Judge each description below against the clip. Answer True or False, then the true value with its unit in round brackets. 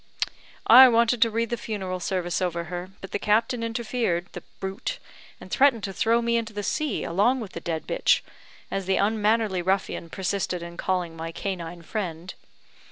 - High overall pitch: True (200 Hz)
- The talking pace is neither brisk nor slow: True (175 wpm)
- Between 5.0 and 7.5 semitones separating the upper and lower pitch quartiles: False (4.4 semitones)